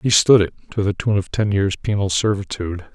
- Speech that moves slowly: No, fast, 205 wpm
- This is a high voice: No, low, 100 Hz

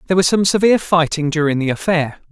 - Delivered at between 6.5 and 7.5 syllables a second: Yes, 6.8 syllables/s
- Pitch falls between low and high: Yes, medium, 165 Hz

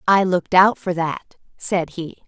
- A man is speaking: No, female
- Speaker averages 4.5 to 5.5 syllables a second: No, 4.2 syllables/s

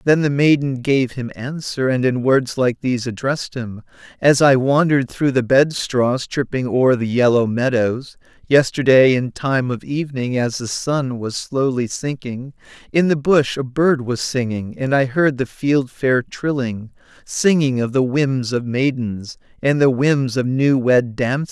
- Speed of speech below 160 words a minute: No, average, 170 wpm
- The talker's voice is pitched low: Yes, low, 130 Hz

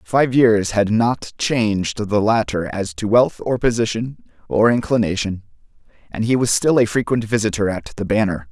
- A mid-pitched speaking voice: No, low, 110 Hz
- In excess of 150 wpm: Yes, average, 170 wpm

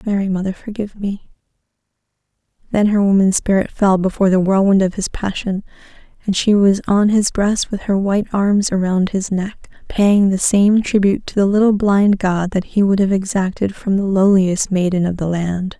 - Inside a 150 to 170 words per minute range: No, average, 185 wpm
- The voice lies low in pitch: No, high, 195 Hz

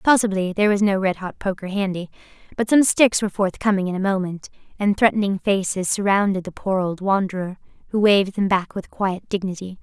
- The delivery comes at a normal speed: Yes, average, 190 wpm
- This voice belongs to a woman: Yes, female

